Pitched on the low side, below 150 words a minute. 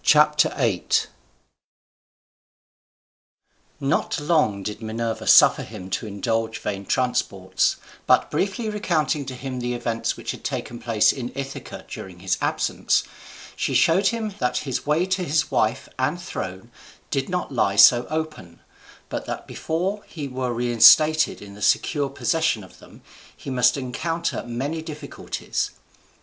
Yes: low, 130 Hz; slow, 135 wpm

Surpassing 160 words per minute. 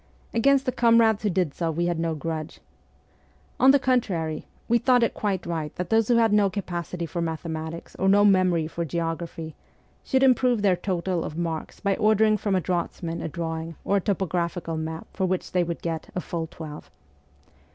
Yes: average, 195 wpm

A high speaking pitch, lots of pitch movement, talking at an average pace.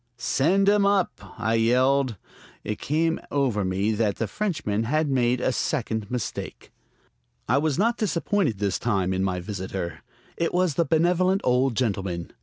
No: low, 125 Hz; wide, 8.0 semitones; average, 155 wpm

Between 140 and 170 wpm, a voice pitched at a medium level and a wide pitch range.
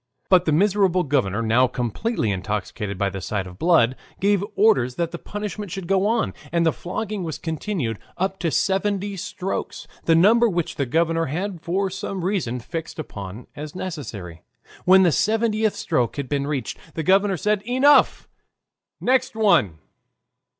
Yes: average, 160 wpm; medium, 170 Hz; wide, 7.7 semitones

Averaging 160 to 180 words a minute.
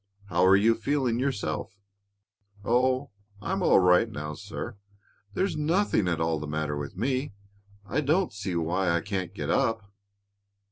No: average, 150 wpm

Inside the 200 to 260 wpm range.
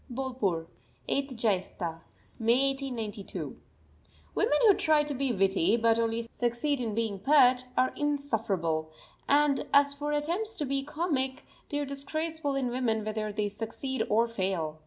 No: average, 145 wpm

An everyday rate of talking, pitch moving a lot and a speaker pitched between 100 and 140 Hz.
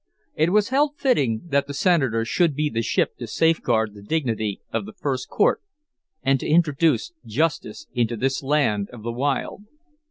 Yes: average, 170 wpm; wide, 6.0 semitones; low, 135 Hz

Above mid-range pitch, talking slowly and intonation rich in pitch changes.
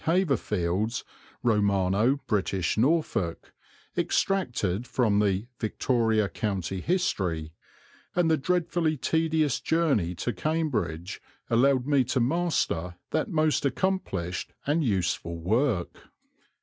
No: low, 115 Hz; slow, 95 wpm; wide, 8.5 semitones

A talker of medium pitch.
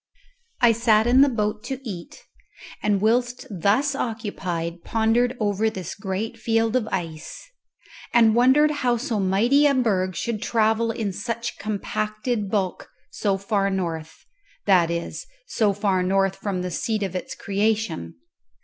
No: high, 215 Hz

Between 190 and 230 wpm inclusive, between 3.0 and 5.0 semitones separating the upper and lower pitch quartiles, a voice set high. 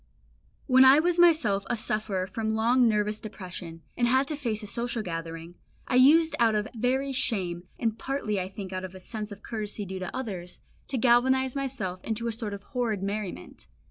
Yes: average, 195 wpm; average, 4.7 semitones; high, 220 Hz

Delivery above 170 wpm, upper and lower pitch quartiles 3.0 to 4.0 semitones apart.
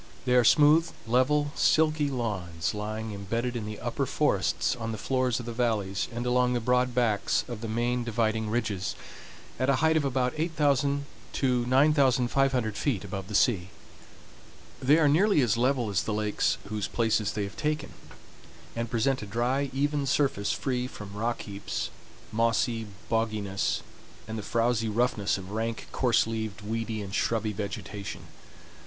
No: average, 160 wpm; average, 3.4 semitones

